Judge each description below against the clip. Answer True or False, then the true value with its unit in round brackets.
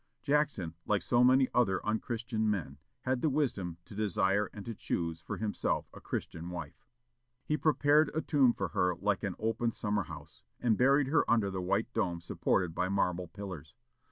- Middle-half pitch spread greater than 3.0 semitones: True (5.4 semitones)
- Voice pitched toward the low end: True (105 Hz)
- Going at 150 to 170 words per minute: False (180 wpm)